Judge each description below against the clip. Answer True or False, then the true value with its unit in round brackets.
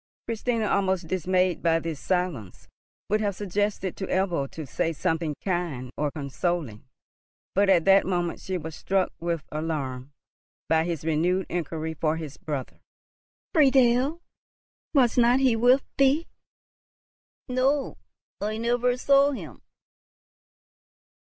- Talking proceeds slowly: True (125 wpm)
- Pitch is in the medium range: True (180 Hz)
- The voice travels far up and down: True (6.3 semitones)